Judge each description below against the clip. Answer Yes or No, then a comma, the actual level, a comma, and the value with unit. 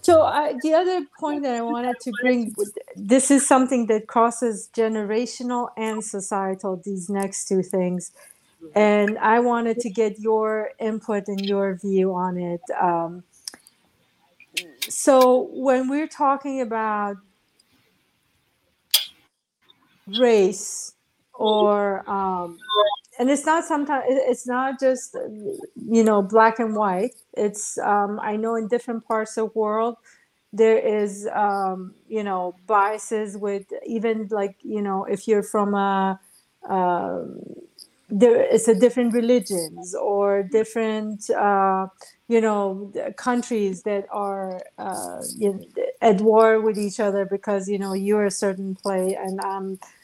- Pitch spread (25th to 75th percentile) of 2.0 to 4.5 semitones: Yes, average, 3.4 semitones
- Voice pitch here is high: Yes, high, 215 Hz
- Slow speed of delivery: Yes, slow, 130 wpm